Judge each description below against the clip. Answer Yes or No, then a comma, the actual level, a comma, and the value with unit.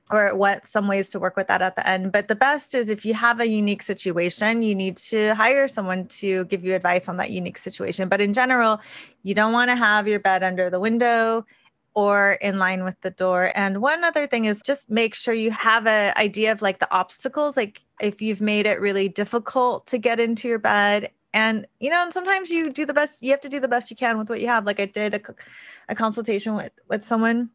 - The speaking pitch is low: No, high, 215 Hz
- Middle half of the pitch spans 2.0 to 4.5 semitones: Yes, average, 3.0 semitones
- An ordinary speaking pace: No, fast, 240 wpm